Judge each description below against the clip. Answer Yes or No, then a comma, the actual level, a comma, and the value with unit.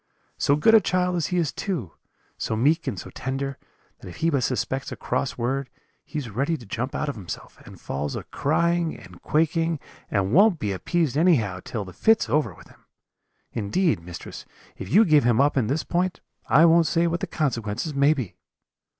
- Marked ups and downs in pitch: Yes, wide, 6.1 semitones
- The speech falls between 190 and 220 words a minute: Yes, average, 200 wpm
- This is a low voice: No, medium, 145 Hz